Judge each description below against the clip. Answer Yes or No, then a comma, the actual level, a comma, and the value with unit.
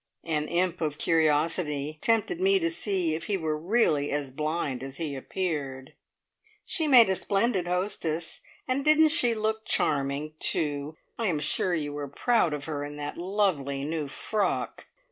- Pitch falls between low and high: Yes, medium, 160 Hz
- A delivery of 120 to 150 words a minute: No, average, 165 wpm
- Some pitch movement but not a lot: No, wide, 5.8 semitones